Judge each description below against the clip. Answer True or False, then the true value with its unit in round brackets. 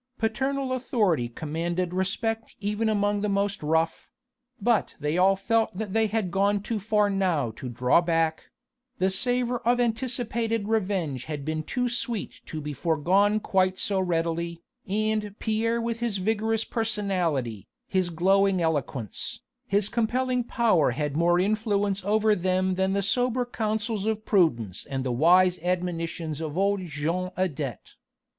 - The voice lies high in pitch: True (195 Hz)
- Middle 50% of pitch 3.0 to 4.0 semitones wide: False (4.8 semitones)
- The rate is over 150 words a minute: False (145 wpm)